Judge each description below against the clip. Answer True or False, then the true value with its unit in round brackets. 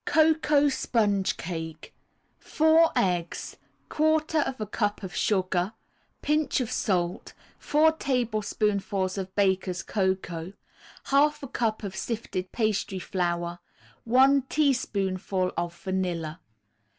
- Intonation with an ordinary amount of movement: False (6.5 semitones)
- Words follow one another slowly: True (100 wpm)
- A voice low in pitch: False (205 Hz)